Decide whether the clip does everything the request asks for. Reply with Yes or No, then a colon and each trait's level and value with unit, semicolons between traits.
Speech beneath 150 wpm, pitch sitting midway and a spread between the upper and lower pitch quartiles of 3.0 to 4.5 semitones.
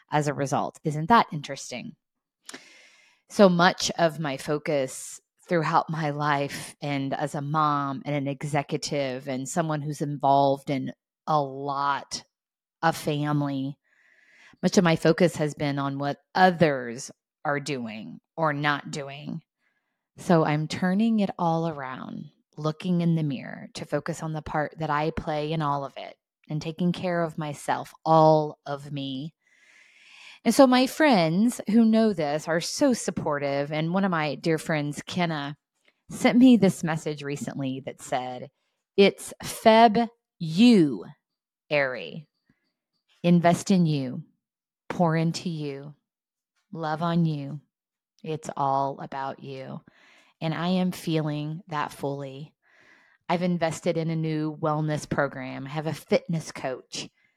Yes: average, 140 wpm; medium, 155 Hz; average, 3.9 semitones